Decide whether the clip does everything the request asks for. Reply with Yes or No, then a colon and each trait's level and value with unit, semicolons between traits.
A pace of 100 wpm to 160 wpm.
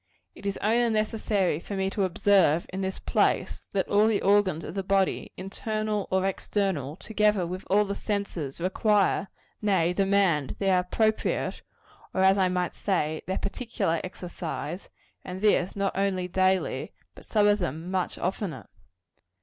Yes: average, 155 wpm